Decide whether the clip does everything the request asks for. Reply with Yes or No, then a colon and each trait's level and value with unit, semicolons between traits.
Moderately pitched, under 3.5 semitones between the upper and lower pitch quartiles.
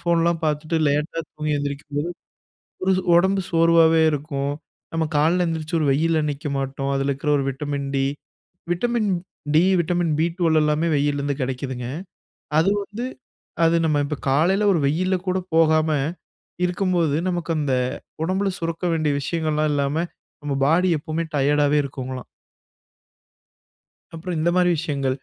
Yes: medium, 155 Hz; average, 3.0 semitones